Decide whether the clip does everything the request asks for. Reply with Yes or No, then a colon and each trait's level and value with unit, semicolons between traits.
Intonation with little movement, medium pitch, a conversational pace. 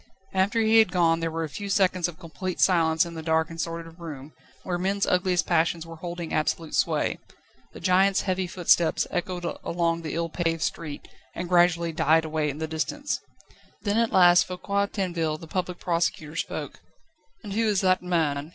Yes: narrow, 2.3 semitones; medium, 170 Hz; average, 185 wpm